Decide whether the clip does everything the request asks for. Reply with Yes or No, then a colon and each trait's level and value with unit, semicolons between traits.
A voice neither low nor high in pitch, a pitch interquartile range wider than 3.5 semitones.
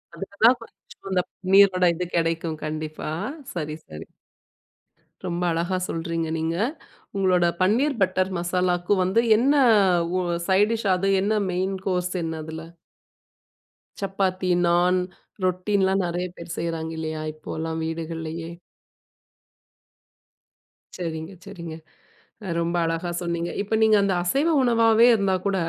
No: medium, 180 Hz; average, 2.9 semitones